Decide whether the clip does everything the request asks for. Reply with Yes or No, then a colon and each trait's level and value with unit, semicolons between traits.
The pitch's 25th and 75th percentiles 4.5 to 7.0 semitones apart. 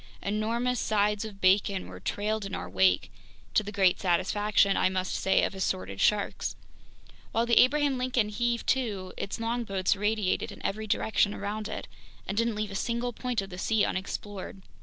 No: average, 2.9 semitones